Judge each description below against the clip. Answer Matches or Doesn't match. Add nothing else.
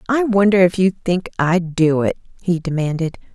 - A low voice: Doesn't match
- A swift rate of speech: Doesn't match